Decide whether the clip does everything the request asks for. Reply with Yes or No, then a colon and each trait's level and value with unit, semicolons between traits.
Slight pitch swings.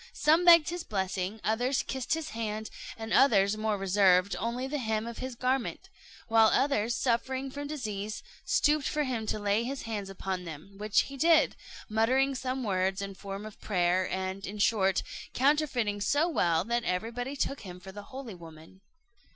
No: average, 5.2 semitones